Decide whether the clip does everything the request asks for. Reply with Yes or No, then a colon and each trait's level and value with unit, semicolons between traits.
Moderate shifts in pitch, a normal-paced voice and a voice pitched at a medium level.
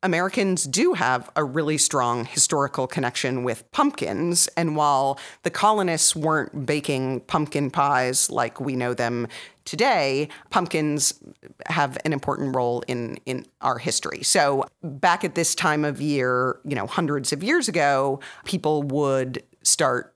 Yes: average, 3.9 semitones; average, 145 wpm; medium, 145 Hz